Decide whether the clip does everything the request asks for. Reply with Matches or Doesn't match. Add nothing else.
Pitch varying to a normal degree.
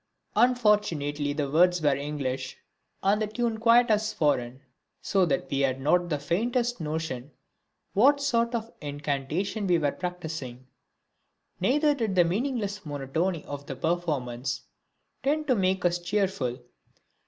Doesn't match